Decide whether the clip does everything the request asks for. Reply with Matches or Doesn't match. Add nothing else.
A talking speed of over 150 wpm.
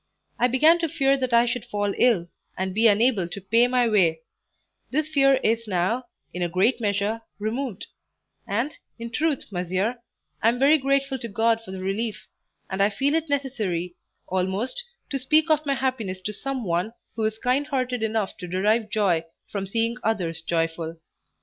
Matches